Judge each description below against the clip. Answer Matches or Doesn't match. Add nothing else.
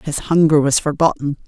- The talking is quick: Doesn't match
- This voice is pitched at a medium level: Matches